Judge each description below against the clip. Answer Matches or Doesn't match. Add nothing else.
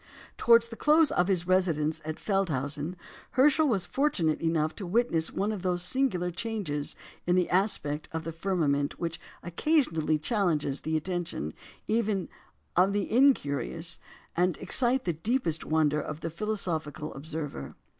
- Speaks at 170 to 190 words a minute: Doesn't match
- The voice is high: Doesn't match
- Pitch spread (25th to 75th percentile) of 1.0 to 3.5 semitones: Doesn't match